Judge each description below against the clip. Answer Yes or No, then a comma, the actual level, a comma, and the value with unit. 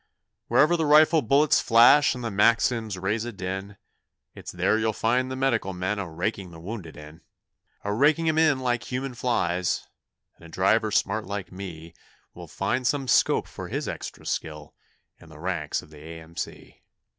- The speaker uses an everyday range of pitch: No, wide, 6.0 semitones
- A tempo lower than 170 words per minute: No, average, 175 wpm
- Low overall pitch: Yes, low, 105 Hz